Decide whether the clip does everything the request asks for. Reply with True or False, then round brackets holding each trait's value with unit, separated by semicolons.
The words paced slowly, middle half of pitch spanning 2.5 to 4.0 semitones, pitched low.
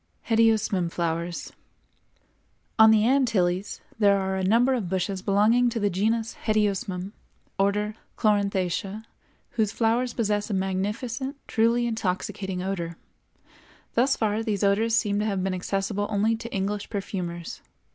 False (130 wpm; 2.8 semitones; 205 Hz)